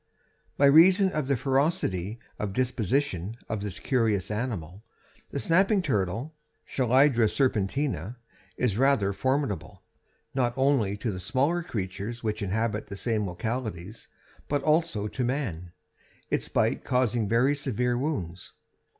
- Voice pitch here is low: Yes, low, 120 Hz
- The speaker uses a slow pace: Yes, slow, 125 wpm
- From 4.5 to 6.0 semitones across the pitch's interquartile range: Yes, average, 5.3 semitones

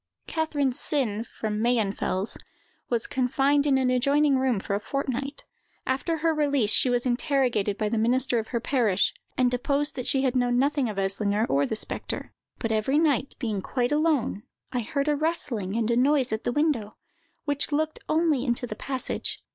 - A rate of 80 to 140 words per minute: No, average, 180 wpm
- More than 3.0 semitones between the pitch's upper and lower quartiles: Yes, average, 4.2 semitones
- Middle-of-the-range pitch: No, very high, 255 Hz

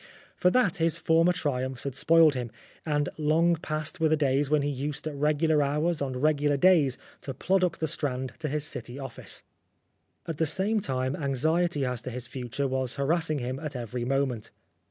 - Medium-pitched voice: Yes, medium, 145 Hz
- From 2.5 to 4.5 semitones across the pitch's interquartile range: Yes, average, 3.5 semitones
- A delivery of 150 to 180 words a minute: No, average, 190 wpm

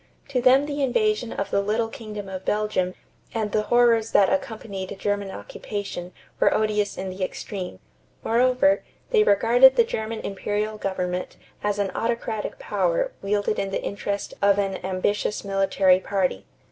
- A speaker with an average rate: Yes, average, 150 wpm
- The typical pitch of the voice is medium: No, high, 210 Hz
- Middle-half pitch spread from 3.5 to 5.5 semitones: No, average, 3.1 semitones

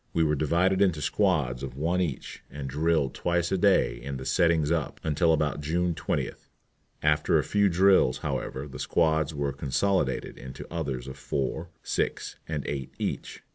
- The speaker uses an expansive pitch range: No, average, 3.7 semitones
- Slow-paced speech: No, average, 170 wpm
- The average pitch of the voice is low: Yes, very low, 80 Hz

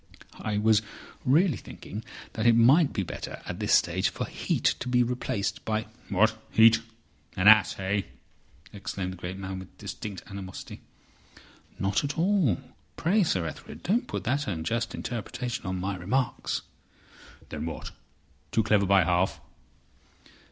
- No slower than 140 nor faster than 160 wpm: Yes, average, 145 wpm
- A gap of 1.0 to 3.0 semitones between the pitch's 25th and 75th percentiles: No, average, 4.4 semitones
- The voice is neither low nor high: No, low, 110 Hz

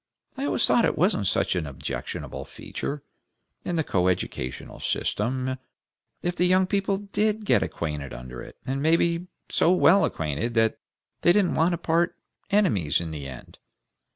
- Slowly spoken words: No, average, 155 wpm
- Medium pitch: Yes, medium, 150 Hz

